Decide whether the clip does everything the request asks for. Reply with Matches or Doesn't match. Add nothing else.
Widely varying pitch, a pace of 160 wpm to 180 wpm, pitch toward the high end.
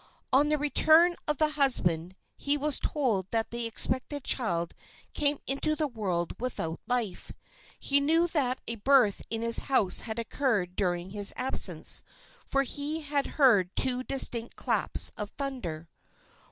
Doesn't match